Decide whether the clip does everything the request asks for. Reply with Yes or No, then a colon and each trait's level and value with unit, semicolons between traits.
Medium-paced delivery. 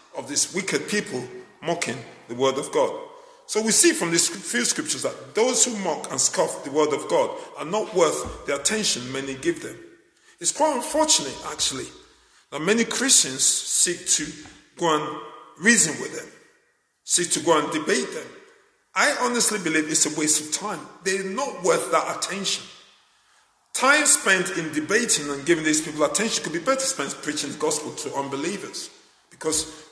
Yes: average, 170 wpm